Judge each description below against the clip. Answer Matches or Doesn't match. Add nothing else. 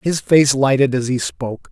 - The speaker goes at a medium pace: Doesn't match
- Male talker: Matches